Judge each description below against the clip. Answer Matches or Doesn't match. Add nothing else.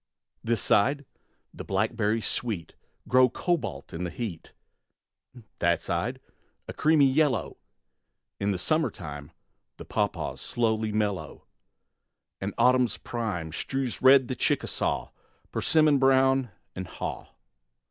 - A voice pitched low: Matches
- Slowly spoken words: Matches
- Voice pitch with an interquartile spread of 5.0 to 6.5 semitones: Matches